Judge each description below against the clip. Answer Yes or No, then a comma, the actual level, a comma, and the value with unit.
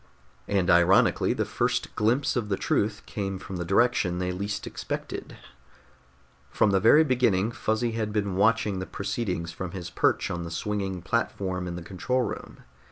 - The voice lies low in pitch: Yes, low, 100 Hz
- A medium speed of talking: Yes, average, 165 wpm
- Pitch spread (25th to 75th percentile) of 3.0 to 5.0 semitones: Yes, average, 3.3 semitones